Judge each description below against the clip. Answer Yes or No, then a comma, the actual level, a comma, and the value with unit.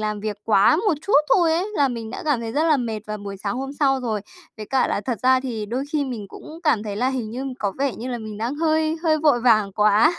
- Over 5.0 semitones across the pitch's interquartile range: Yes, wide, 5.4 semitones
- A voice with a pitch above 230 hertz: Yes, very high, 250 Hz